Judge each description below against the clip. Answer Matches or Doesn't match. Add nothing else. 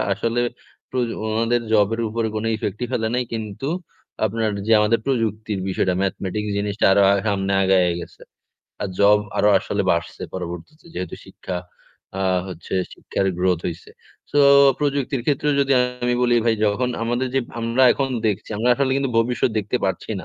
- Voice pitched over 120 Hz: Doesn't match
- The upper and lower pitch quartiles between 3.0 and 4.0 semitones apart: Matches